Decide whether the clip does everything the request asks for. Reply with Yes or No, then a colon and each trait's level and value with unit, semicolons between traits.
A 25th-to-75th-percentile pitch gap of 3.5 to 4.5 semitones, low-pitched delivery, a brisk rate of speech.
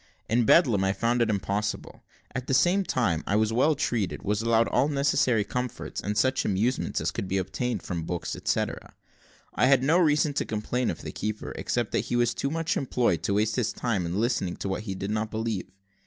Yes: average, 4.1 semitones; low, 115 Hz; fast, 215 wpm